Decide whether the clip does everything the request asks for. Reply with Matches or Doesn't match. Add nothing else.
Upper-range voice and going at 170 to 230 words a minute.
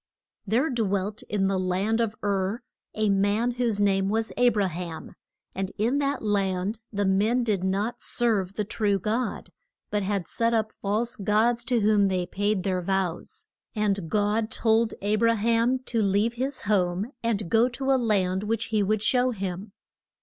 Matches